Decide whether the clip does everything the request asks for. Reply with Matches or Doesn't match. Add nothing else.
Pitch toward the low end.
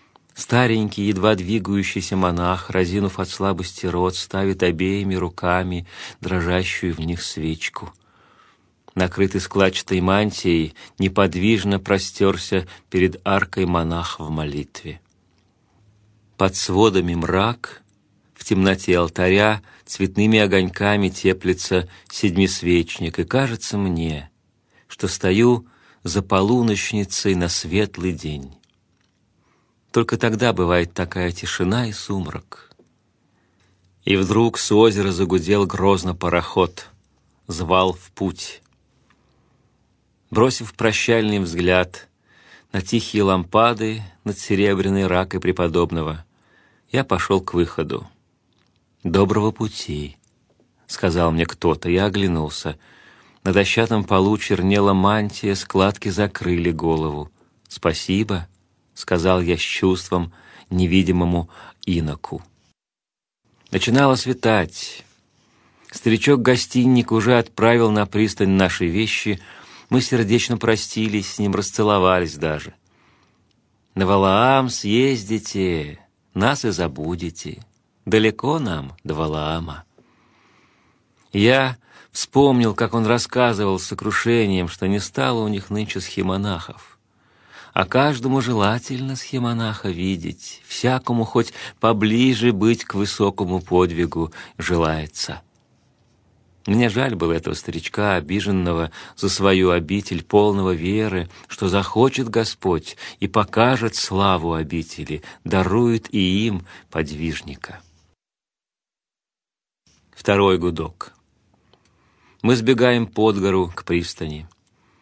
Matches